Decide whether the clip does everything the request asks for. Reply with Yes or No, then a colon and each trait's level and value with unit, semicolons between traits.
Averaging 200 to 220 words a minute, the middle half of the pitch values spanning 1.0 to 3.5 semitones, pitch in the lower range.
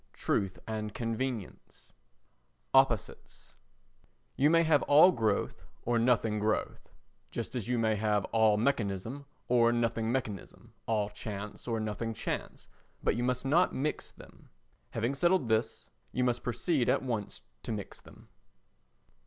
No: average, 145 wpm; average, 3.2 semitones; low, 115 Hz